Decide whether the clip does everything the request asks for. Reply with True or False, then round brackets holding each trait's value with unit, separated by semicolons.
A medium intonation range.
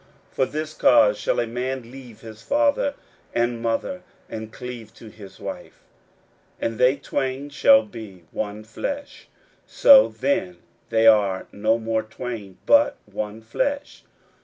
False (5.9 semitones)